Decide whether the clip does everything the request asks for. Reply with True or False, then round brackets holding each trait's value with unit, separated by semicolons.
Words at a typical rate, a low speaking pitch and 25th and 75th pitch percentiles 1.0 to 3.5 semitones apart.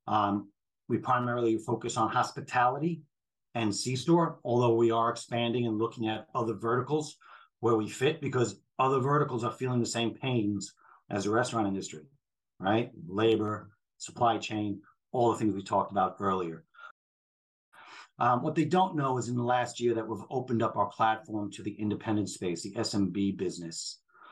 True (165 wpm; 115 Hz; 3.1 semitones)